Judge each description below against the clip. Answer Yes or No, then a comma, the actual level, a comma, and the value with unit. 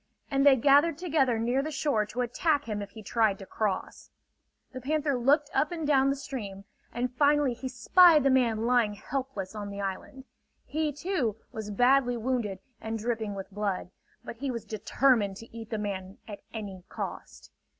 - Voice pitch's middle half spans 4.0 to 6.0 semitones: Yes, average, 4.7 semitones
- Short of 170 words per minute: No, average, 180 wpm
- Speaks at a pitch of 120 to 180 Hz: No, high, 245 Hz